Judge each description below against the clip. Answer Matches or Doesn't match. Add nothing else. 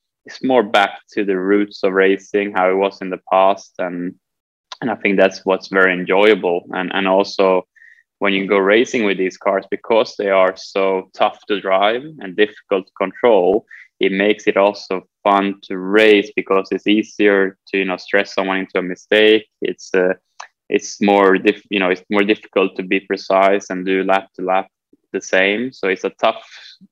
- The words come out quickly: Doesn't match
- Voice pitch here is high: Doesn't match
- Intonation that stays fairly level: Matches